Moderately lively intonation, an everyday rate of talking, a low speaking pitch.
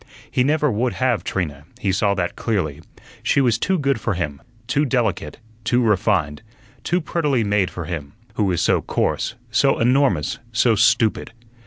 No: wide, 5.8 semitones; average, 165 wpm; low, 110 Hz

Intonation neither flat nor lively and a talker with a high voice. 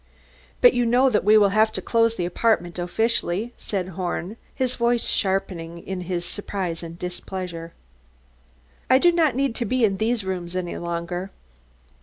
Yes: average, 4.8 semitones; high, 195 Hz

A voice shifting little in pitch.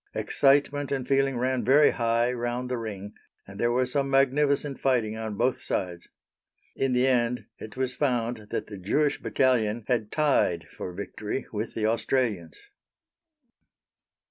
No: average, 3.6 semitones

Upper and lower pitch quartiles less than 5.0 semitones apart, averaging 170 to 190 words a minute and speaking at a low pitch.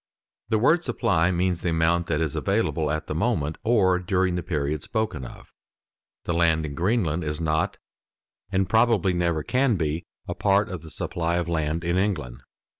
Yes: average, 3.6 semitones; average, 180 wpm; very low, 85 Hz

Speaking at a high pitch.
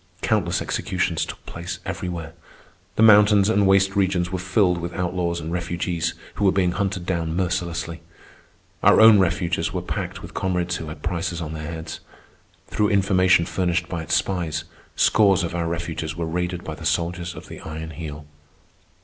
No: very low, 90 Hz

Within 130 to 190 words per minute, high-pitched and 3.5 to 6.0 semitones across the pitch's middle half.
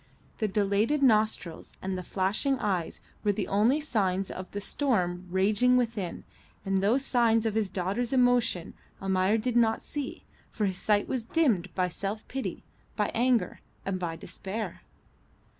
Yes: average, 155 wpm; high, 210 Hz; average, 4.2 semitones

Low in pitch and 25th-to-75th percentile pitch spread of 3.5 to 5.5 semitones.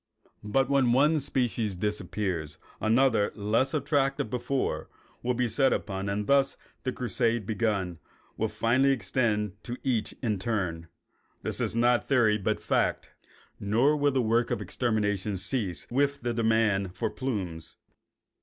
Yes: low, 115 Hz; average, 4.0 semitones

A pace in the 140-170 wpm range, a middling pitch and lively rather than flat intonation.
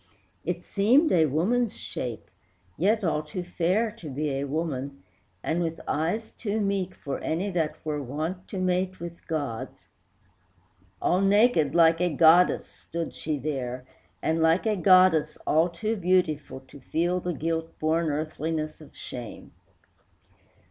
No: average, 145 wpm; medium, 165 Hz; average, 3.3 semitones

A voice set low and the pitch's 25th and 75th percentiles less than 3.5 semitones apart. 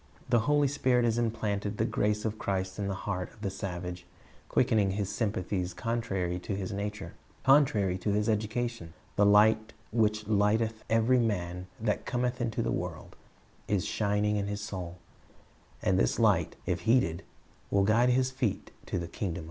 Yes: low, 105 Hz; average, 2.8 semitones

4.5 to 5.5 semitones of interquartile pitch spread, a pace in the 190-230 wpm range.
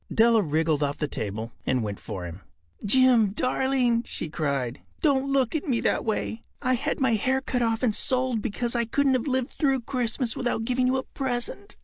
Yes: average, 5.1 semitones; average, 200 wpm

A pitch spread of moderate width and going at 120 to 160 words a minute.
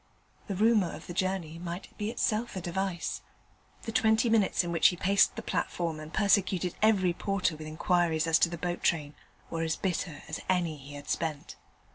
No: average, 3.3 semitones; average, 190 wpm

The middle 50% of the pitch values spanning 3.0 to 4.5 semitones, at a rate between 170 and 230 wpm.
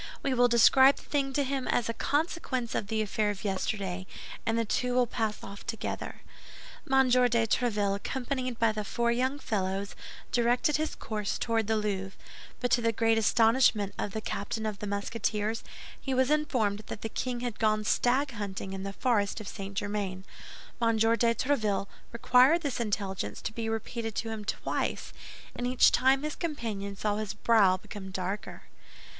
Yes: average, 3.4 semitones; average, 175 wpm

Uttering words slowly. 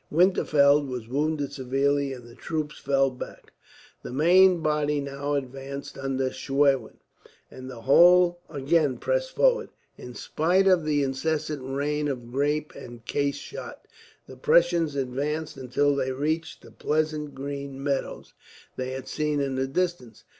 No: average, 145 wpm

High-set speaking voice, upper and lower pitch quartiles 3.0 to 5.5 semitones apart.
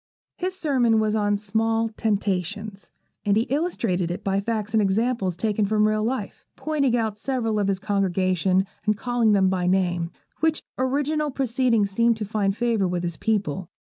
Yes: high, 215 Hz; average, 3.3 semitones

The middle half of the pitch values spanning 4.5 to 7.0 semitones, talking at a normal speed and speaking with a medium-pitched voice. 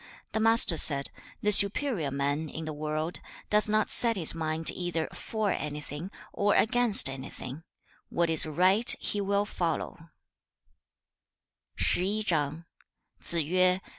No: average, 5.2 semitones; slow, 110 wpm; medium, 170 Hz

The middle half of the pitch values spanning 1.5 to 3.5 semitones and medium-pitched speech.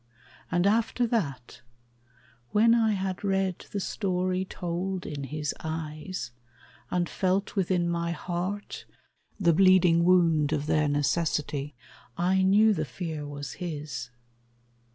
No: average, 3.9 semitones; medium, 175 Hz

